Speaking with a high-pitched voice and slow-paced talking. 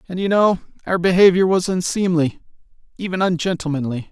No: medium, 175 Hz; slow, 130 wpm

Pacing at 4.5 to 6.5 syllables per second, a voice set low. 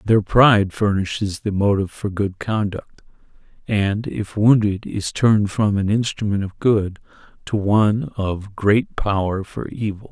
No: 4.3 syllables/s; low, 105 Hz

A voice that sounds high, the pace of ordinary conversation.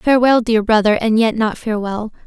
Yes: high, 220 Hz; average, 160 wpm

